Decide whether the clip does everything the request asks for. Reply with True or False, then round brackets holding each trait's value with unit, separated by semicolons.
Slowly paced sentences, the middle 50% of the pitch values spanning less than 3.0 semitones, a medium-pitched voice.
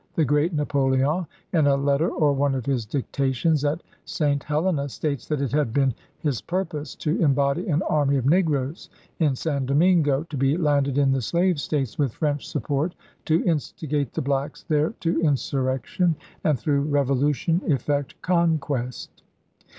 False (160 wpm; 2.5 semitones; 145 Hz)